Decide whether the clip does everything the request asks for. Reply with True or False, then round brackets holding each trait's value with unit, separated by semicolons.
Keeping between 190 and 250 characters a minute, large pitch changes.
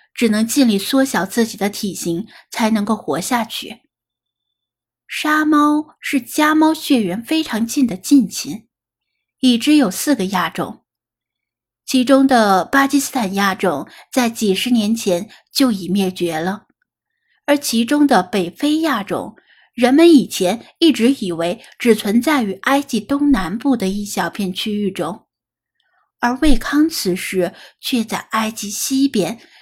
True (200 characters per minute; 6.5 semitones)